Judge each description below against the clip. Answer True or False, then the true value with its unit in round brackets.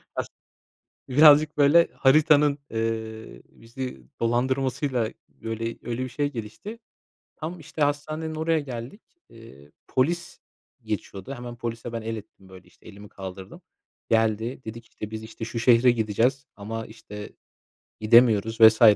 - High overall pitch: False (115 Hz)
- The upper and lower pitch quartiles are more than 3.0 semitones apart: True (4.1 semitones)